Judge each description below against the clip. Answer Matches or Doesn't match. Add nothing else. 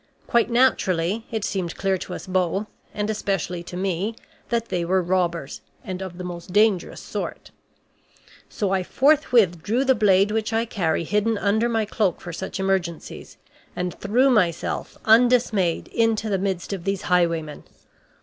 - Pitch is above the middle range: Matches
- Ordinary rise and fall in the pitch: Matches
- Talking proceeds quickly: Doesn't match